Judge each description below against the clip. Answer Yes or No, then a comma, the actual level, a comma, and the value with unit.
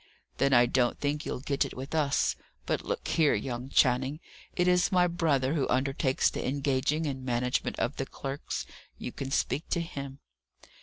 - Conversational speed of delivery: Yes, average, 175 wpm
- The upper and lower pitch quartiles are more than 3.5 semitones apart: No, narrow, 2.6 semitones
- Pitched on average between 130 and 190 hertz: Yes, low, 135 Hz